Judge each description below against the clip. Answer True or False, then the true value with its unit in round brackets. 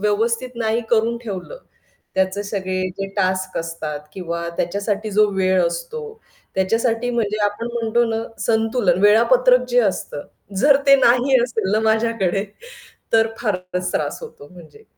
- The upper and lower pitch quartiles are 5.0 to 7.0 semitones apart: False (3.8 semitones)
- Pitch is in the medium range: False (215 Hz)